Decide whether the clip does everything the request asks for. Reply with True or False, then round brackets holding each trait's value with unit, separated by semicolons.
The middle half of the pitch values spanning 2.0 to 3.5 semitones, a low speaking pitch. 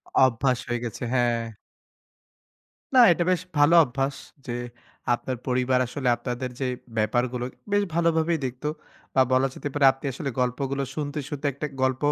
True (2.8 semitones; 130 Hz)